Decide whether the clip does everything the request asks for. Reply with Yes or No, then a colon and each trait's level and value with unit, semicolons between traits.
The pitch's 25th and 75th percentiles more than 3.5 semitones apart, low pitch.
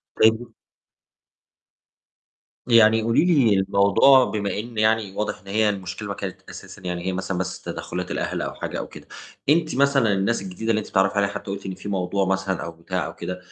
No: average, 2.8 semitones; low, 100 Hz